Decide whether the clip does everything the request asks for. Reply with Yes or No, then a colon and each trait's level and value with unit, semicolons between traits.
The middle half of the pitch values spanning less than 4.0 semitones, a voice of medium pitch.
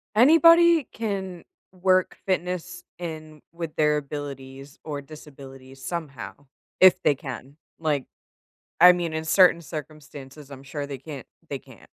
No: average, 4.4 semitones; medium, 155 Hz